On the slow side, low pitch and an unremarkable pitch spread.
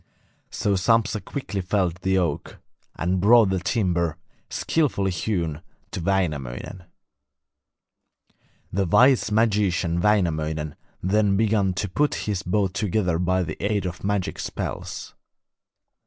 Yes: slow, 115 wpm; very low, 95 Hz; average, 3.2 semitones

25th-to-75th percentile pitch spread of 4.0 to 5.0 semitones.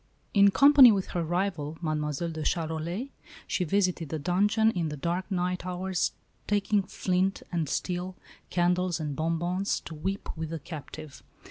No: average, 3.1 semitones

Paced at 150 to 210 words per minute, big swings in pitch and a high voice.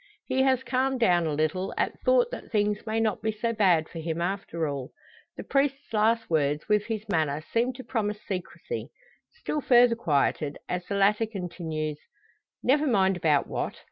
Yes: average, 175 wpm; wide, 6.2 semitones; high, 210 Hz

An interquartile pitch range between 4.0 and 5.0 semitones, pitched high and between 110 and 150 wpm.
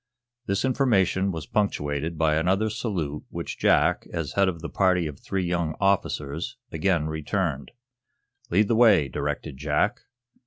No: average, 4.3 semitones; very low, 85 Hz; average, 145 wpm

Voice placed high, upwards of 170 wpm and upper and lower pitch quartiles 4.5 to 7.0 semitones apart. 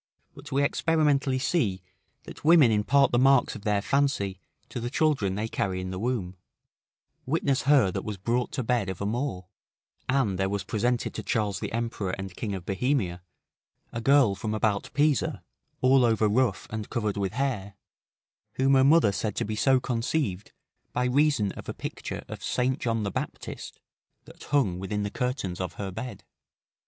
No: low, 115 Hz; average, 180 wpm; average, 5.2 semitones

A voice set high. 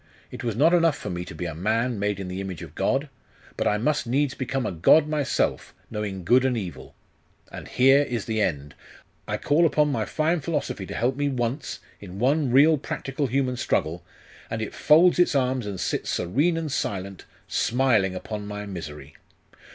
No: low, 120 Hz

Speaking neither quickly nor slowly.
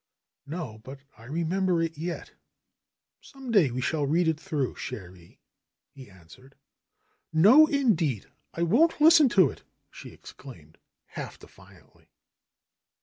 No: slow, 125 wpm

